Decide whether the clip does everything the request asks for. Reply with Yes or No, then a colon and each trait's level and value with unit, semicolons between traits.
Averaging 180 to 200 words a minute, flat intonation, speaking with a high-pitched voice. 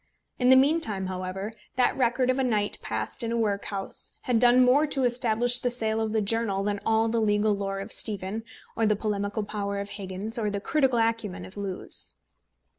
No: average, 195 wpm; average, 3.3 semitones; high, 220 Hz